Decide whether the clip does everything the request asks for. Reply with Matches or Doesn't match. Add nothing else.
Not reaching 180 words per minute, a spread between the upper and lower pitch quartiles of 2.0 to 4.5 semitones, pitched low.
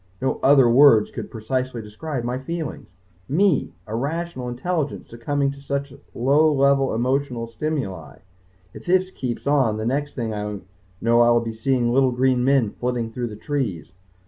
Matches